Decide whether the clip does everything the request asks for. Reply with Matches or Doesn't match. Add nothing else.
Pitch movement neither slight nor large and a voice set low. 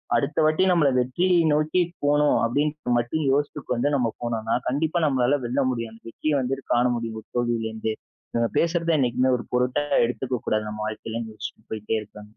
Matches